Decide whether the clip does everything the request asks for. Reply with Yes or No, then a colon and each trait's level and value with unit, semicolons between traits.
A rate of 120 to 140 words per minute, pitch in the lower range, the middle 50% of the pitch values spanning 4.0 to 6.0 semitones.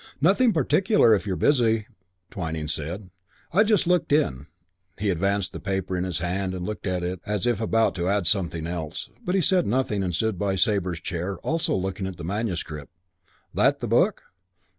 No: average, 185 wpm; very low, 95 Hz; average, 4.3 semitones